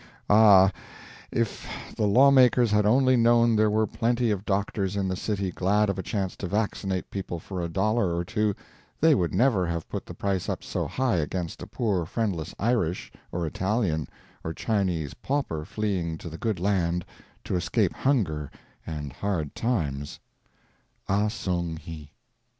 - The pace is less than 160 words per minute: No, average, 165 wpm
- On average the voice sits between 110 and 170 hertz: No, low, 100 Hz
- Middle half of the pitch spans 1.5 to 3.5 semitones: No, average, 4.3 semitones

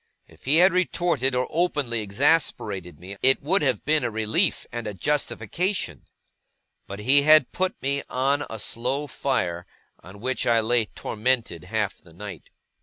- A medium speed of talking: Yes, average, 160 wpm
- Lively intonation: Yes, wide, 5.7 semitones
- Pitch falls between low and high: No, low, 125 Hz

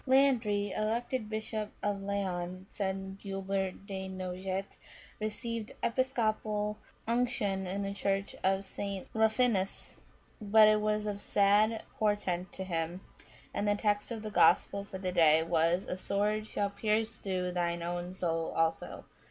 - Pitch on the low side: No, high, 200 Hz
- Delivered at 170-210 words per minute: No, average, 145 wpm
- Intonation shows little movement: Yes, narrow, 2.3 semitones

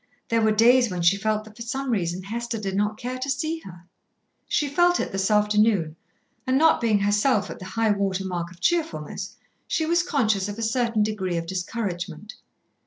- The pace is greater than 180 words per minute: Yes, average, 195 wpm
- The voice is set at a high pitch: Yes, high, 215 Hz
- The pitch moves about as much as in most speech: Yes, average, 4.1 semitones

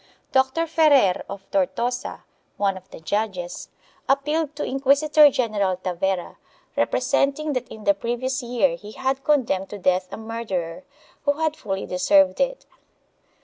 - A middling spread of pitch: No, wide, 6.5 semitones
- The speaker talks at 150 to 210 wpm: No, average, 140 wpm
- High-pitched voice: Yes, high, 245 Hz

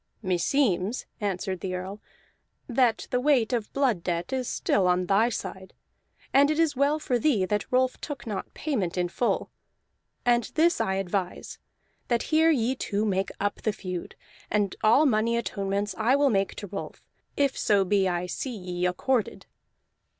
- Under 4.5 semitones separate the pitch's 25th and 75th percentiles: No, wide, 5.4 semitones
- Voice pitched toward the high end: Yes, high, 215 Hz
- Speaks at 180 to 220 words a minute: No, average, 165 wpm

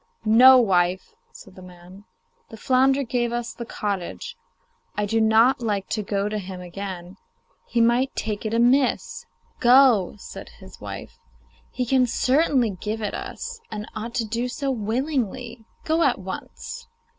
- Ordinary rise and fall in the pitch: Yes, average, 4.0 semitones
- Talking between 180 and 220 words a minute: No, average, 155 wpm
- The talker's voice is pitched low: No, high, 230 Hz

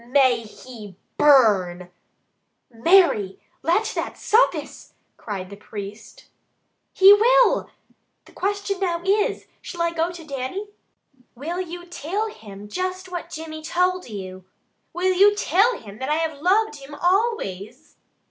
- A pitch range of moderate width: No, wide, 8.7 semitones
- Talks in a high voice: Yes, very high, 330 Hz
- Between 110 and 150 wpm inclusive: Yes, slow, 135 wpm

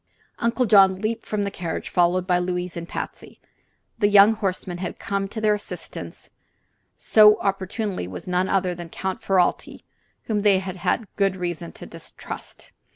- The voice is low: No, high, 190 Hz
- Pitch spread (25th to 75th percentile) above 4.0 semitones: No, narrow, 2.5 semitones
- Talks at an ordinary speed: Yes, average, 165 wpm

